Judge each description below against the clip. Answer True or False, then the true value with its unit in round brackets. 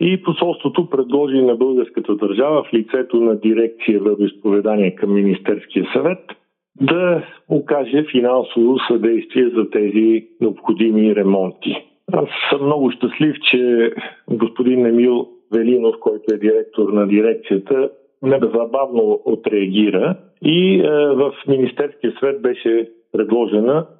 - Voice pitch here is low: True (120 Hz)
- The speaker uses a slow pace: True (110 wpm)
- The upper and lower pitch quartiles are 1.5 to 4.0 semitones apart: False (4.5 semitones)